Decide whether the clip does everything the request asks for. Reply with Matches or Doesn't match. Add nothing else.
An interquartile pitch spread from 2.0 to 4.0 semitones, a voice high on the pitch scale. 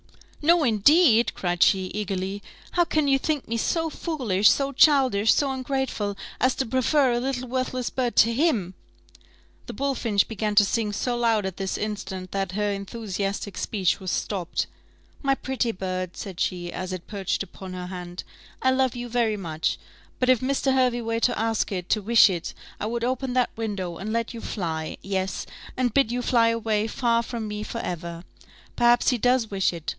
Doesn't match